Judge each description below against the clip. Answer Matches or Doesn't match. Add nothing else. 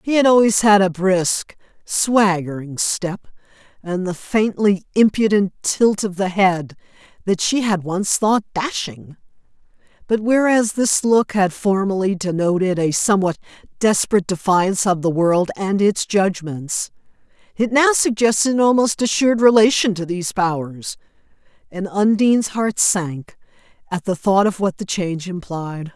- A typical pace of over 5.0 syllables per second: Doesn't match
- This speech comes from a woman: Matches